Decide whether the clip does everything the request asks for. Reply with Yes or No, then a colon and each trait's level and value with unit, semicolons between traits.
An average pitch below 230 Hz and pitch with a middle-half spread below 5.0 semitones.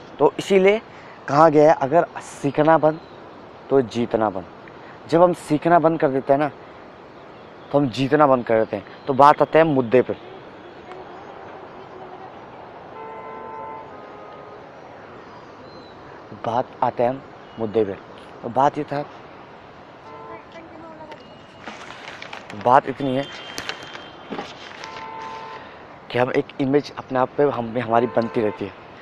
Yes: low, 135 Hz; average, 3.8 semitones